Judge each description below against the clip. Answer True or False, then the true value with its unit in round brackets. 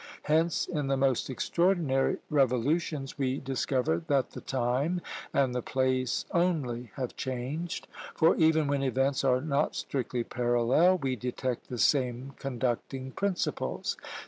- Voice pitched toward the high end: False (135 Hz)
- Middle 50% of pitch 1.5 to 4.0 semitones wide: True (3.1 semitones)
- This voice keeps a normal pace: False (130 wpm)